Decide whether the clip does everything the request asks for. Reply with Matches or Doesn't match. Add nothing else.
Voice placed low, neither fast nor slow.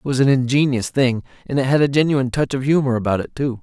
Doesn't match